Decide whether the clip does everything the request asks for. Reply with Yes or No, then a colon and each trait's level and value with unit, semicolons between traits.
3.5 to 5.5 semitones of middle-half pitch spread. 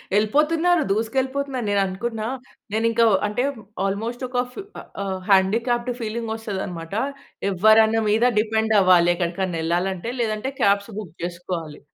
Yes: average, 3.9 semitones